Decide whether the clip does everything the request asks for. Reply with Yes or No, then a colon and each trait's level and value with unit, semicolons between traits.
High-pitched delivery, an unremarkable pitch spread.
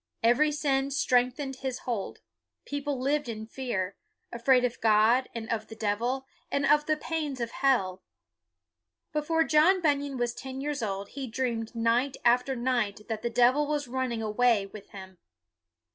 Yes: very high, 250 Hz; average, 3.6 semitones